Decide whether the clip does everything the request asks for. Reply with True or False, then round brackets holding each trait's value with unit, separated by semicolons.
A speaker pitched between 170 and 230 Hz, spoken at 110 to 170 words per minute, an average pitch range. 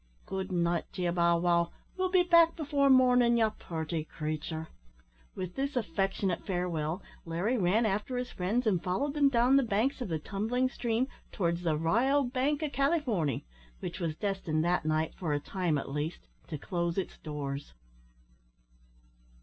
False (190 Hz; 165 wpm; 7.2 semitones)